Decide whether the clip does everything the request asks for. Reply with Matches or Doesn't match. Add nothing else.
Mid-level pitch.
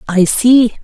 Doesn't match